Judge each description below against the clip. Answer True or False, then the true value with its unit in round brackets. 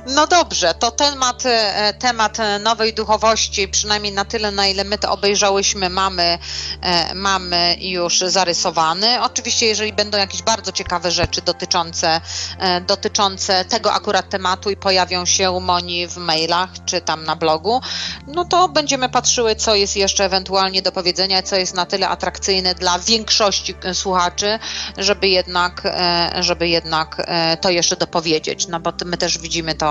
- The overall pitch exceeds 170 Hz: True (190 Hz)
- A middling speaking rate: True (145 wpm)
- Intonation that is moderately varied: True (3.0 semitones)